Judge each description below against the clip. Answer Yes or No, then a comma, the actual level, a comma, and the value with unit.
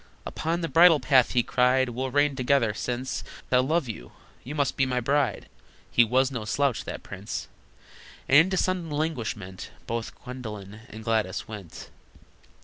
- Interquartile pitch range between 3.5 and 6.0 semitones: Yes, average, 4.2 semitones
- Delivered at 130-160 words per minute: Yes, average, 155 wpm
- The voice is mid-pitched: No, low, 125 Hz